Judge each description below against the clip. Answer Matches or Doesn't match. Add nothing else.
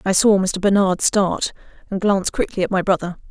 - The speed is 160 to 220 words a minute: Matches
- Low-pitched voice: Doesn't match